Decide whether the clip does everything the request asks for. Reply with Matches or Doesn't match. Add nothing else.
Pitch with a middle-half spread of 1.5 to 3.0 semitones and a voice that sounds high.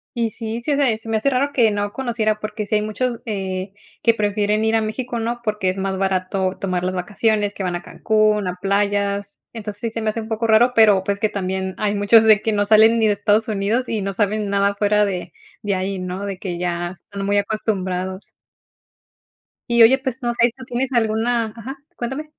Matches